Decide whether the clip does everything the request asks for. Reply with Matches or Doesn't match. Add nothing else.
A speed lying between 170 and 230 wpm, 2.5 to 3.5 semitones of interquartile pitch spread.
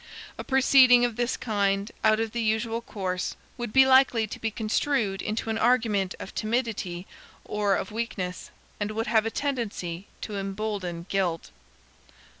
Doesn't match